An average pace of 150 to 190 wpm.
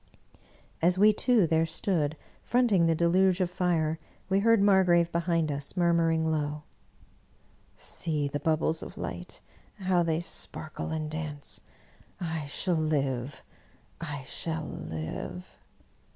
No: slow, 135 wpm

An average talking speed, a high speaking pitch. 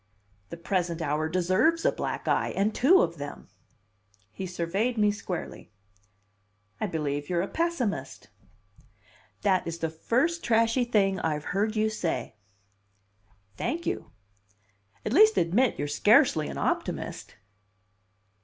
No: slow, 125 wpm; high, 195 Hz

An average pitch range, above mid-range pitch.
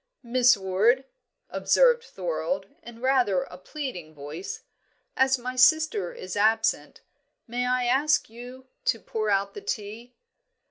Yes: average, 4.5 semitones; high, 240 Hz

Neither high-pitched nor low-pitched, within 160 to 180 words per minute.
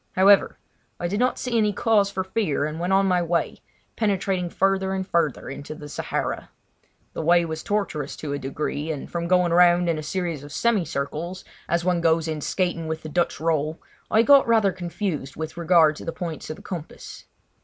No: medium, 170 Hz; average, 200 wpm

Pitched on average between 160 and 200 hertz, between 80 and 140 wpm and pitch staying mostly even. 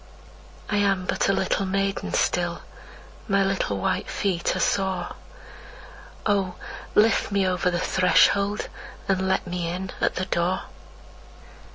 Yes: high, 190 Hz; slow, 135 wpm; narrow, 1.5 semitones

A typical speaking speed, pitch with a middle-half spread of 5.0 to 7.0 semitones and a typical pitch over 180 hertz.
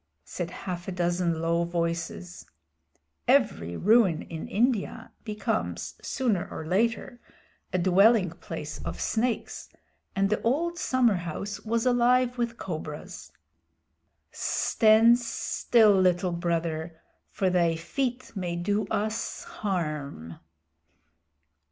No: slow, 105 wpm; average, 5.3 semitones; high, 190 Hz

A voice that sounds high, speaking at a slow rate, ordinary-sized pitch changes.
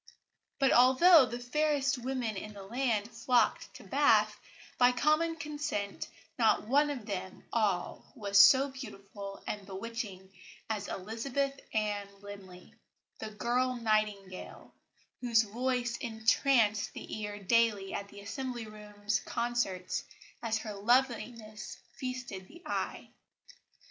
Yes: high, 225 Hz; slow, 120 wpm; average, 3.8 semitones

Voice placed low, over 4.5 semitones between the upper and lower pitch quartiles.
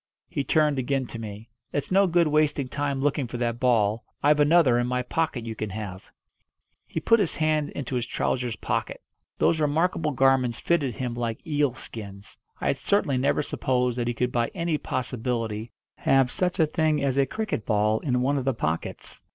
No: low, 130 Hz; average, 4.2 semitones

